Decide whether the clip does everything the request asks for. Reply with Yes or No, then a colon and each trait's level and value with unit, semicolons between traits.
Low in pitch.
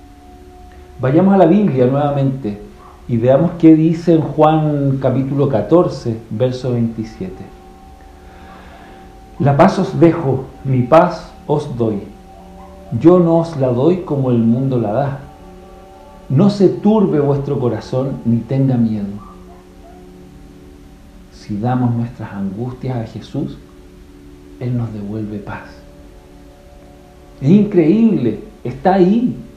Yes: low, 120 Hz